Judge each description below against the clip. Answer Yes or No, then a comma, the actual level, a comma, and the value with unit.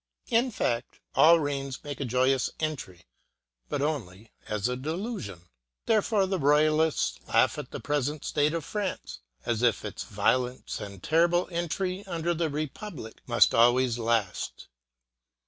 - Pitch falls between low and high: Yes, medium, 145 Hz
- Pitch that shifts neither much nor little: No, wide, 6.0 semitones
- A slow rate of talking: No, average, 145 wpm